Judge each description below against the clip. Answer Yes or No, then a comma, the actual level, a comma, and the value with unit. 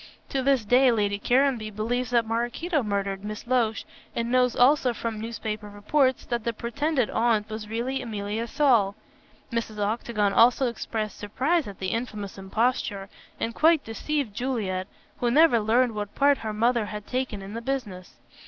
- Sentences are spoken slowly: No, average, 160 wpm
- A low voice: No, high, 230 Hz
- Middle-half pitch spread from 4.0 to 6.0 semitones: No, average, 3.2 semitones